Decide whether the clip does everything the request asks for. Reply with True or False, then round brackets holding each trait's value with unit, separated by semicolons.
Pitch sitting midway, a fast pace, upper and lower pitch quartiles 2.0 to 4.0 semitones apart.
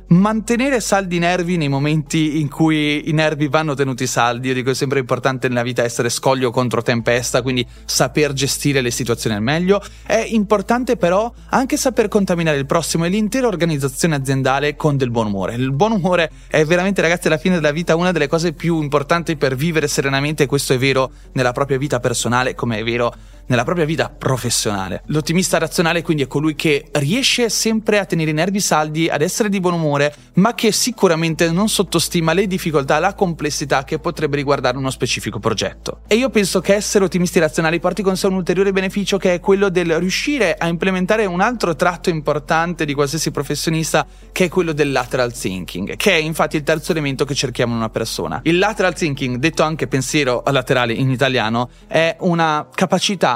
False (155 Hz; 190 wpm; 5.2 semitones)